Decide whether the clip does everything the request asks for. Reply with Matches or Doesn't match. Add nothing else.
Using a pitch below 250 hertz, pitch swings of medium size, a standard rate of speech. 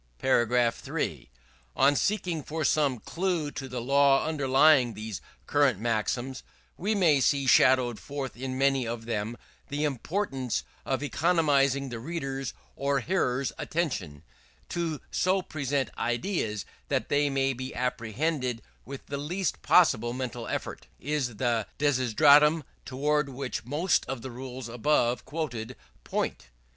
Doesn't match